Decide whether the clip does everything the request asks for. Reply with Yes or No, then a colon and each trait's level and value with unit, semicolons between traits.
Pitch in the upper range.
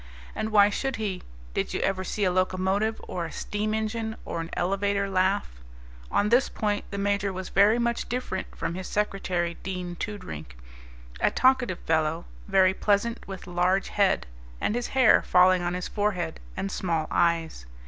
Yes: high, 195 Hz